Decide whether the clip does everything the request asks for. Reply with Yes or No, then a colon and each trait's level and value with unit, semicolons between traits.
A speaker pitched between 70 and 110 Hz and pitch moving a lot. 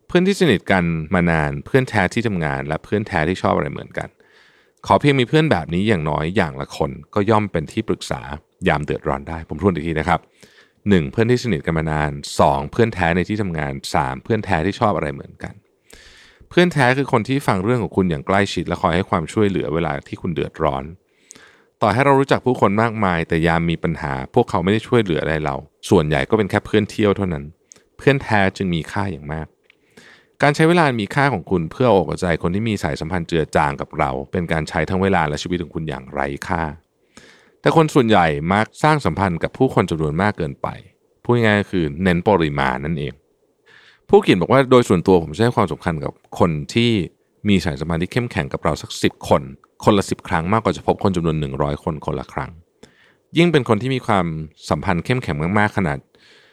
Yes: very low, 95 Hz; wide, 5.8 semitones